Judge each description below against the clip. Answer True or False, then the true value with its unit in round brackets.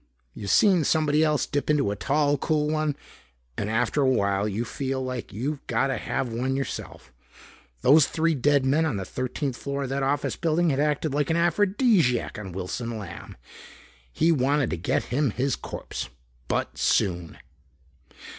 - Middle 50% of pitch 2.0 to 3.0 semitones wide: False (4.3 semitones)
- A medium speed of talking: True (170 wpm)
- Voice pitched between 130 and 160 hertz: True (135 Hz)